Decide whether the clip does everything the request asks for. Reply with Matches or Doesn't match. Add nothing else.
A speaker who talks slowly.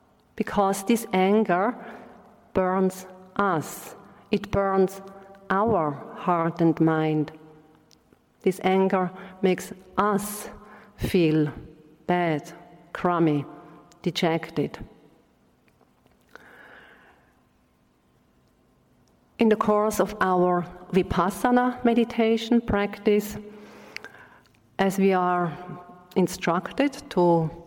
Matches